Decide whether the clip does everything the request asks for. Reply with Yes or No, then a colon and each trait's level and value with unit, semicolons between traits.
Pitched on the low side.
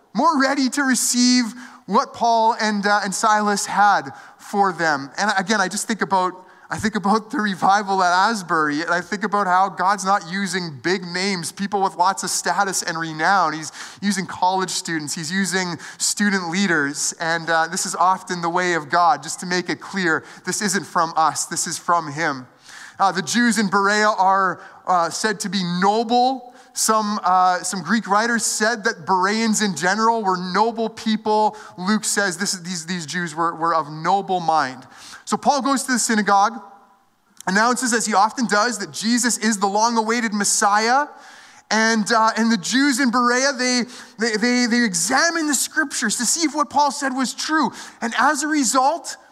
No: high, 205 Hz